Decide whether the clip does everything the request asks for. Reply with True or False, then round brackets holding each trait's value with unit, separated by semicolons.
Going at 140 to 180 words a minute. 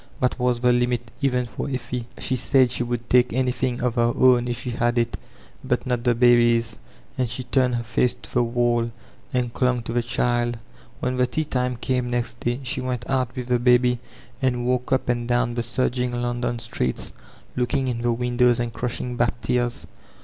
False (200 wpm)